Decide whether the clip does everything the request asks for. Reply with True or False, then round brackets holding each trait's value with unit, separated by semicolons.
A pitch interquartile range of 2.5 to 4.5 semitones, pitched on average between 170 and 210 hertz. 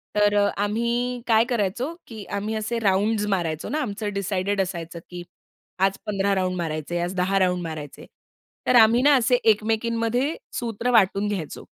True (3.8 semitones; 205 Hz)